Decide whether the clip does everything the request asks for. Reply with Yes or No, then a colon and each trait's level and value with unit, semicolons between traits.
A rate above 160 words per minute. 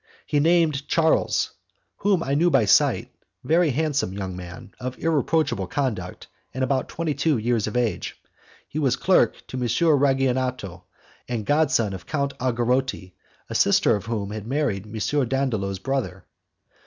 No: average, 155 wpm